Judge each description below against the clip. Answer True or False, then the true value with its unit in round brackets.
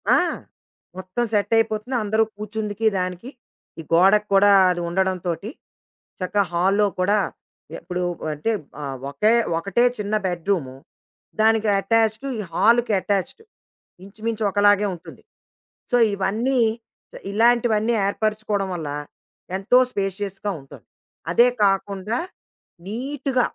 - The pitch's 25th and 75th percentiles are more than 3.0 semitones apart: False (2.7 semitones)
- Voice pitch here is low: False (205 Hz)